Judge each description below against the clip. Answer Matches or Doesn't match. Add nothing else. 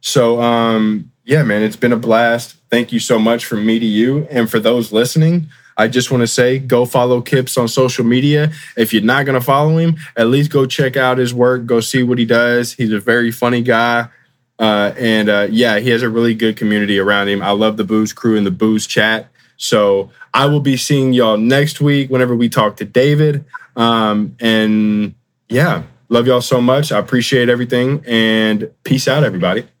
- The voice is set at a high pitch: Doesn't match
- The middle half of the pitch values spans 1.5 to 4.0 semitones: Matches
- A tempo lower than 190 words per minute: Doesn't match